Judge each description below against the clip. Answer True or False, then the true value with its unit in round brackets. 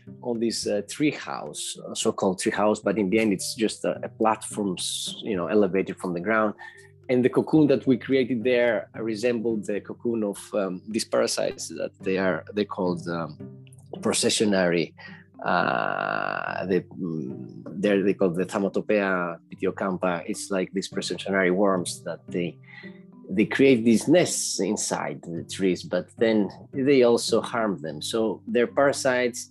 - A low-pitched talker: True (105 Hz)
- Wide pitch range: False (4.2 semitones)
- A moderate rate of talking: True (155 wpm)